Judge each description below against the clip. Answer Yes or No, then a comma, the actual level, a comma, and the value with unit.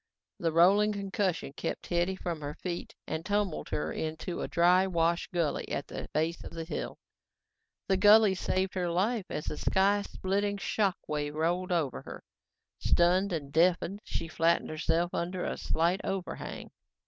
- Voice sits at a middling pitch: Yes, medium, 175 Hz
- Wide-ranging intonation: No, average, 2.7 semitones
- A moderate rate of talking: Yes, average, 160 wpm